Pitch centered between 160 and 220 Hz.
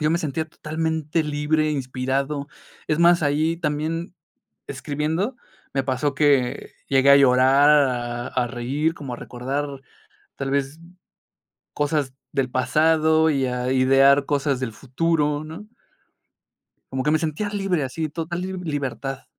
No: medium, 145 Hz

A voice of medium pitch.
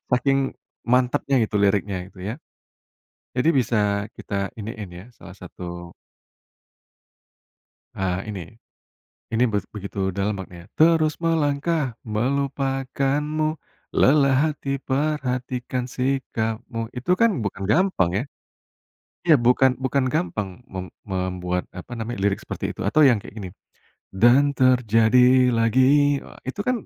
No: low, 120 Hz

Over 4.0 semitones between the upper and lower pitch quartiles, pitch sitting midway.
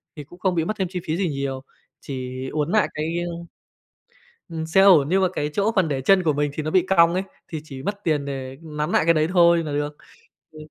No: average, 3.6 semitones; medium, 160 Hz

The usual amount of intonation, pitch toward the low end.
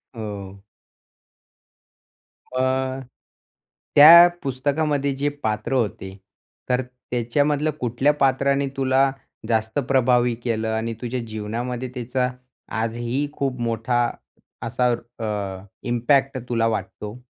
Yes: average, 3.0 semitones; low, 125 Hz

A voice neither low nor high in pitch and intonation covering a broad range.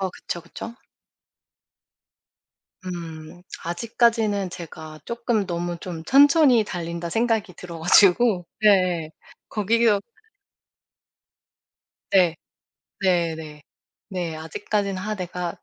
No: medium, 180 Hz; average, 4.0 semitones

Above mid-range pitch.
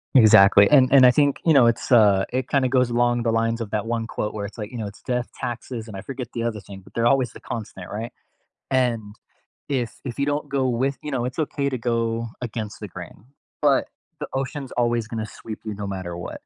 No: low, 120 Hz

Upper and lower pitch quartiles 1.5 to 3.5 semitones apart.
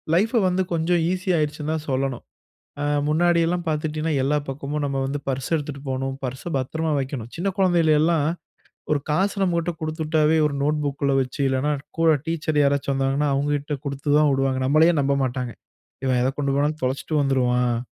Yes: average, 2.9 semitones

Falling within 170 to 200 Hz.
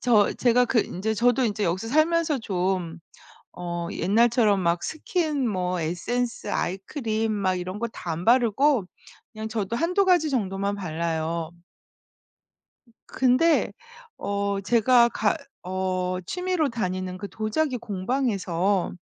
No: high, 215 Hz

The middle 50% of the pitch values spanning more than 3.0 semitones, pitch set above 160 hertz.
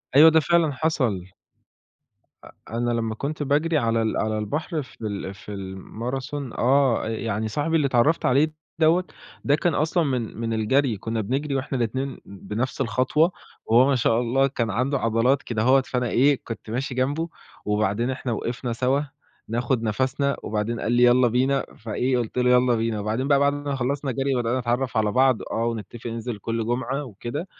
No: average, 3.4 semitones; low, 125 Hz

